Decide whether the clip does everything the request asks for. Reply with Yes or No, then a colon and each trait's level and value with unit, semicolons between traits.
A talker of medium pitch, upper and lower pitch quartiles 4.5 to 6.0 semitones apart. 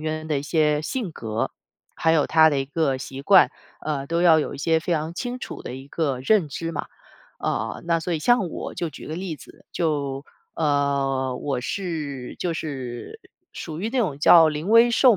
No: medium, 155 Hz; average, 3.4 semitones